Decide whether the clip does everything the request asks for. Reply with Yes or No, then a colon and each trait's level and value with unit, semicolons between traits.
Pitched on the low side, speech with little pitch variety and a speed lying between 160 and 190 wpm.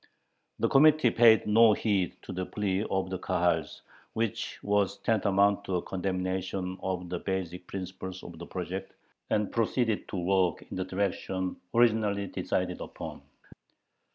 No: very low, 95 Hz; narrow, 2.2 semitones; average, 145 wpm